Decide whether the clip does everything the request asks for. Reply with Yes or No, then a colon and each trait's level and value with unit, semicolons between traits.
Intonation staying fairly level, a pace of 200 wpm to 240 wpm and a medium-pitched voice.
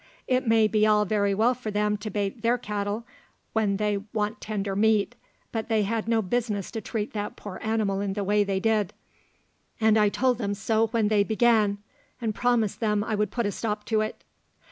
No: narrow, 1.5 semitones; fast, 205 wpm; high, 215 Hz